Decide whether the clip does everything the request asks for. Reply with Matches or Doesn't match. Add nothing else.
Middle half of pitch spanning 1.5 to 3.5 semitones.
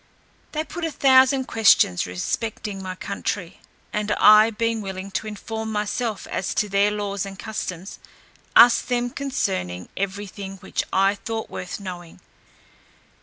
Matches